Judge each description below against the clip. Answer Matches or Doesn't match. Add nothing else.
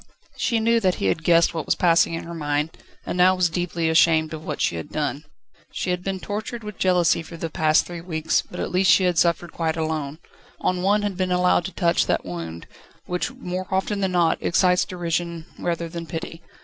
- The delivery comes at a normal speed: Doesn't match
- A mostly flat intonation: Matches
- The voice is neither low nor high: Matches